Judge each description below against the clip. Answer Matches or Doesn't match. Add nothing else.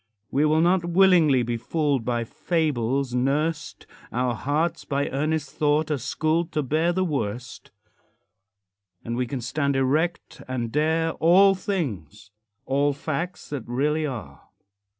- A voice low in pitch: Doesn't match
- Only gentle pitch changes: Doesn't match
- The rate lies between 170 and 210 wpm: Doesn't match